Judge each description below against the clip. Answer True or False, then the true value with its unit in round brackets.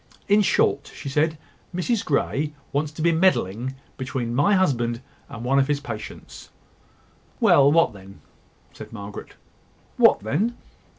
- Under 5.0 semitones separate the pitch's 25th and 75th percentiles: False (5.5 semitones)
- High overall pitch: False (140 Hz)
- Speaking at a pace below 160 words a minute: True (135 wpm)